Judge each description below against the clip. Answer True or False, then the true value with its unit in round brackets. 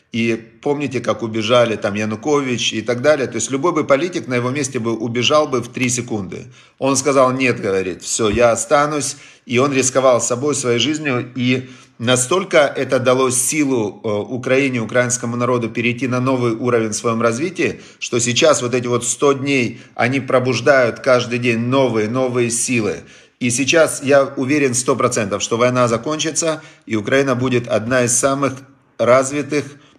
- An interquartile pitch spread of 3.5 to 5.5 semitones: False (2.4 semitones)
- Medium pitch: False (125 Hz)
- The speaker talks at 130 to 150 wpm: False (160 wpm)